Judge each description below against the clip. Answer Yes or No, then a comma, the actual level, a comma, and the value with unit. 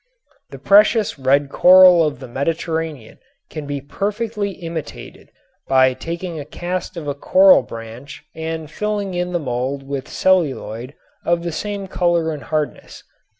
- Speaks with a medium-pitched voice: Yes, medium, 160 Hz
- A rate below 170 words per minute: Yes, average, 145 wpm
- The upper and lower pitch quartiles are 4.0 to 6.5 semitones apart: Yes, average, 4.7 semitones